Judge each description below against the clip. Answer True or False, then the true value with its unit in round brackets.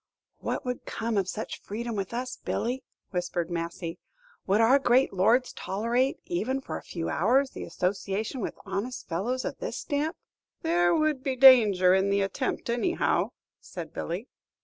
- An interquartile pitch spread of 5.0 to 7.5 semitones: True (5.4 semitones)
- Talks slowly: False (160 wpm)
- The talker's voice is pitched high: True (225 Hz)